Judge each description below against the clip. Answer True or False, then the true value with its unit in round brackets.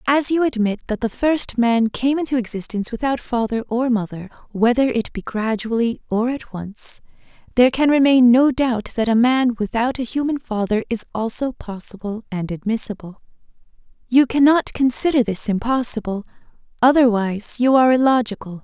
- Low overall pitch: False (240 Hz)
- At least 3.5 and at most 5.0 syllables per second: False (5.2 syllables/s)